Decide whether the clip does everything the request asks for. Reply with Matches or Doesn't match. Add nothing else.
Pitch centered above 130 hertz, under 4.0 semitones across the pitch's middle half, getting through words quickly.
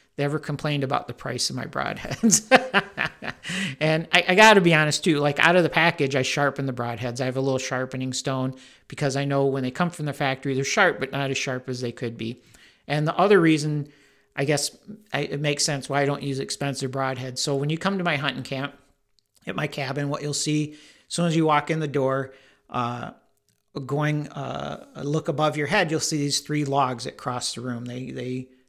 Matches